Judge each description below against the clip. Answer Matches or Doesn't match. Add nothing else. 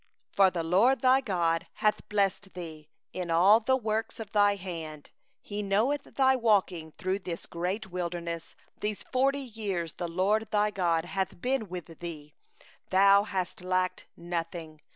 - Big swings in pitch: Doesn't match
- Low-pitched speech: Doesn't match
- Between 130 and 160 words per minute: Matches